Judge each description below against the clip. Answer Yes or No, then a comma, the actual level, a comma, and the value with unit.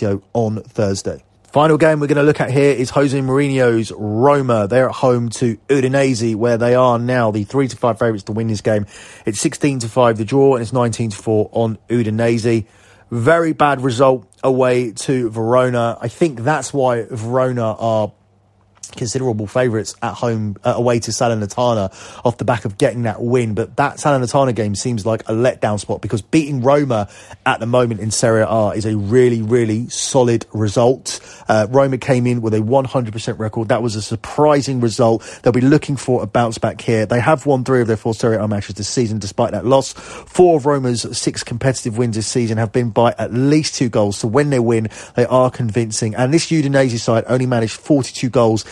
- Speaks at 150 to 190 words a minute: No, average, 200 wpm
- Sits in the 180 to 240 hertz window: No, low, 120 Hz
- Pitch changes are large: No, average, 2.9 semitones